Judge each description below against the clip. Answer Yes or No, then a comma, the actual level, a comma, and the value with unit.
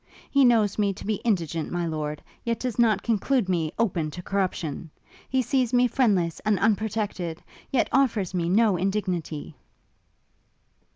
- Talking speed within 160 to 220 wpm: No, average, 150 wpm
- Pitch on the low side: No, high, 200 Hz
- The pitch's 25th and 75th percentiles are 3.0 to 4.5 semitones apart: No, average, 5.1 semitones